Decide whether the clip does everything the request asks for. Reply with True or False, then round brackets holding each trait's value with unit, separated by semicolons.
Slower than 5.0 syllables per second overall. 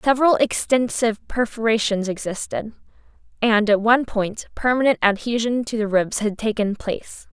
False (5.1 syllables/s)